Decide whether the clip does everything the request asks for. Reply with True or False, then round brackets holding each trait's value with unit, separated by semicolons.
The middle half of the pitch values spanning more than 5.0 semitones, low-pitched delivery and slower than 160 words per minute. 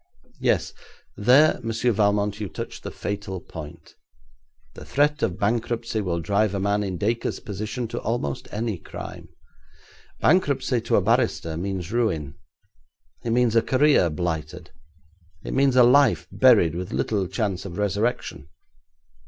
False (4.5 semitones; 105 Hz; 140 wpm)